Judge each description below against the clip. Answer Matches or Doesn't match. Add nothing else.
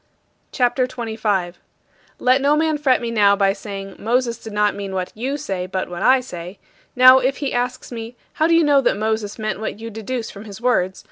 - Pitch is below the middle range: Doesn't match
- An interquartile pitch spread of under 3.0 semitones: Doesn't match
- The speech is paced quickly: Matches